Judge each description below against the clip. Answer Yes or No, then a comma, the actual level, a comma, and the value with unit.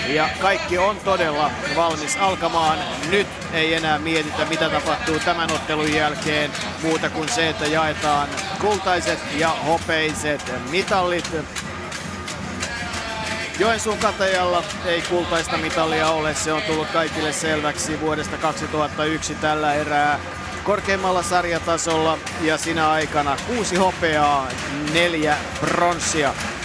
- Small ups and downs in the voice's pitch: Yes, narrow, 2.3 semitones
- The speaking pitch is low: No, medium, 160 Hz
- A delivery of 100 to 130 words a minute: Yes, average, 110 wpm